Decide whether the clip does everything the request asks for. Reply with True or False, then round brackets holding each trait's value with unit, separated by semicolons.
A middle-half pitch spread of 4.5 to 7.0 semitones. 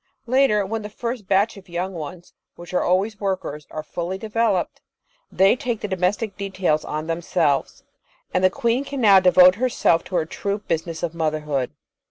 False (3.8 semitones)